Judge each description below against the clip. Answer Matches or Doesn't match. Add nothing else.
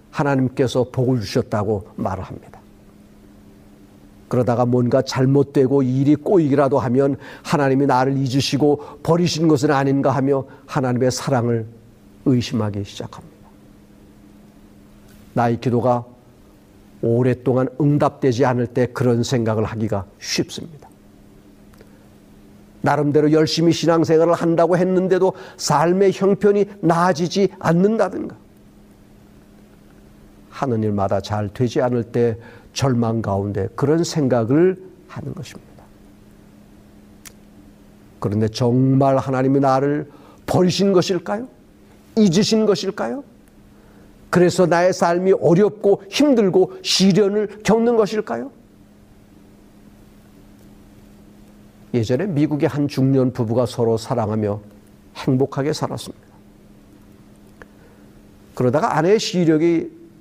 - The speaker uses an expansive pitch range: Matches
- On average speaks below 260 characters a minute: Matches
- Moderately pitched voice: Doesn't match